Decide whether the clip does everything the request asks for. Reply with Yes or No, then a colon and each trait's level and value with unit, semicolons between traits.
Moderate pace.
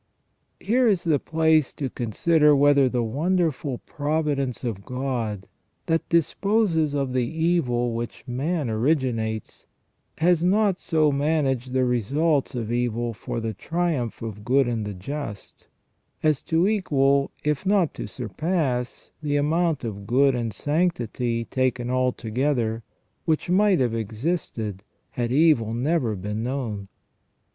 No: slow, 130 wpm